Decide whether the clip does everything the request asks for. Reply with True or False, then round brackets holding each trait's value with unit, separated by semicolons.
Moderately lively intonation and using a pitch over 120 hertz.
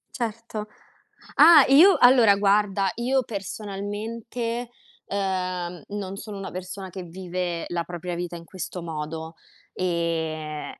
True (3.7 semitones; 190 Hz)